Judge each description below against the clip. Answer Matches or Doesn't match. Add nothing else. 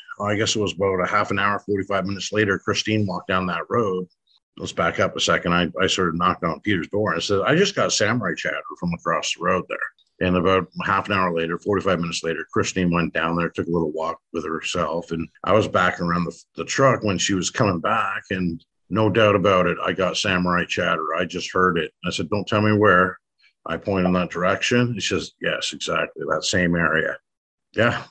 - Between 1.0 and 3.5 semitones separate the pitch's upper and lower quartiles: Matches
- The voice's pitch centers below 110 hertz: Matches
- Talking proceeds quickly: Matches